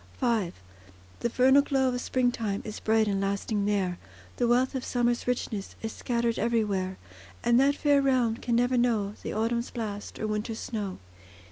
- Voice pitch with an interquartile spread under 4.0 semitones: Yes, average, 2.9 semitones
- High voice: Yes, high, 230 Hz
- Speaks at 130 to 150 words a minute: No, average, 165 wpm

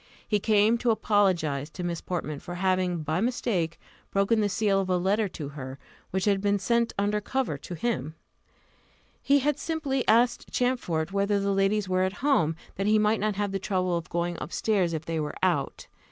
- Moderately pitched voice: No, high, 195 Hz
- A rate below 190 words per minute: No, average, 195 wpm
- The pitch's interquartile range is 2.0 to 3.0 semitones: No, average, 3.8 semitones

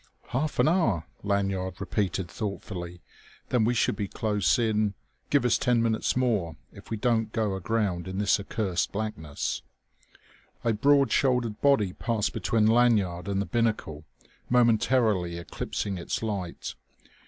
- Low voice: Yes, low, 105 Hz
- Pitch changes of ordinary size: Yes, average, 3.5 semitones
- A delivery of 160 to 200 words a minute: No, average, 140 wpm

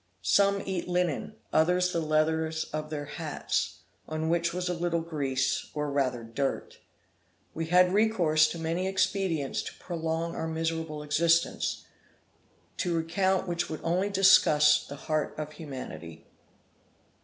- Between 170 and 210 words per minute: No, slow, 135 wpm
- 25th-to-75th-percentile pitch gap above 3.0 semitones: No, narrow, 2.6 semitones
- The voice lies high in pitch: No, medium, 160 Hz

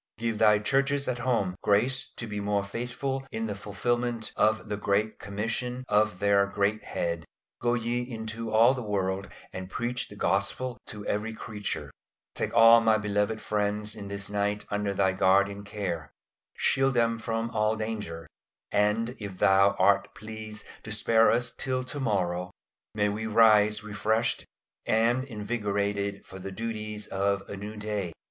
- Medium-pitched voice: No, low, 105 Hz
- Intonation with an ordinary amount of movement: No, narrow, 2.3 semitones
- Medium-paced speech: Yes, average, 155 wpm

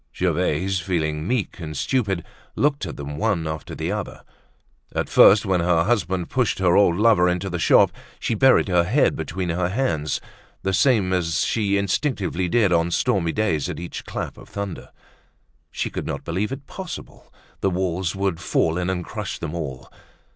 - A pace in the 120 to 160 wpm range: No, average, 175 wpm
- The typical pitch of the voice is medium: No, very low, 90 Hz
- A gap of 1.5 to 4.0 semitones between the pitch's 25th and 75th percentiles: Yes, average, 3.4 semitones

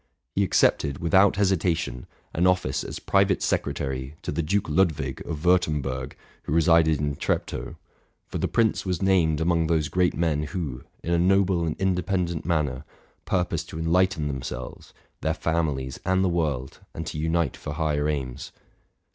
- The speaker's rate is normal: Yes, average, 165 wpm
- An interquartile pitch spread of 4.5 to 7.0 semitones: No, average, 3.7 semitones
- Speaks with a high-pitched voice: No, very low, 80 Hz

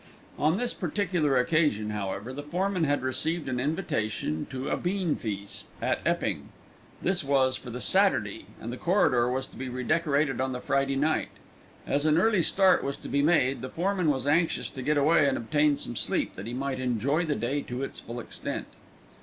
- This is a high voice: No, medium, 140 Hz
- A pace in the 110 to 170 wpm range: No, average, 190 wpm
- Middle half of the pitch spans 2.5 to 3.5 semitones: No, average, 4.3 semitones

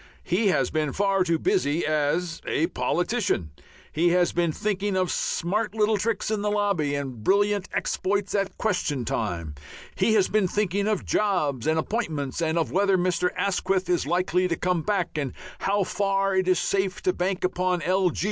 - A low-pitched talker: No, medium, 185 Hz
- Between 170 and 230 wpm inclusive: Yes, average, 175 wpm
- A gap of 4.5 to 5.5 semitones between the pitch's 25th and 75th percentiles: No, average, 3.5 semitones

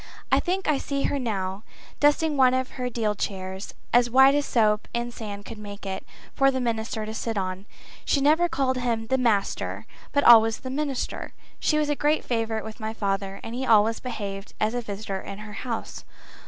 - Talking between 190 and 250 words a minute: Yes, average, 200 wpm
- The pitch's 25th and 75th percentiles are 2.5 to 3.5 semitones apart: No, average, 4.1 semitones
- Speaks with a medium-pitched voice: No, high, 230 Hz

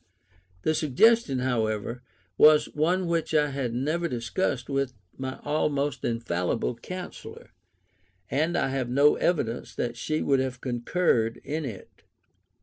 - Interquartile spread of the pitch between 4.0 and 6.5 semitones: Yes, average, 4.3 semitones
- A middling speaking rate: No, slow, 130 wpm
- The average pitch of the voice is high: No, low, 135 Hz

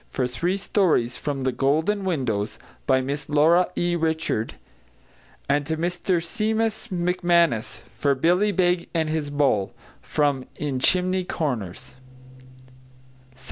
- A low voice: No, medium, 160 Hz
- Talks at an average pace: No, slow, 125 wpm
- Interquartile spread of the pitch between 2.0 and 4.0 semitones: No, average, 5.1 semitones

